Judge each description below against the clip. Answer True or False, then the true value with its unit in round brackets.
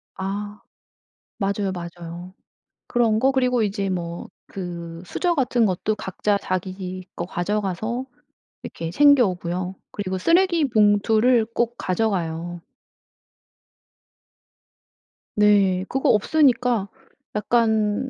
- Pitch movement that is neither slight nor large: True (4.4 semitones)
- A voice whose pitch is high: True (205 Hz)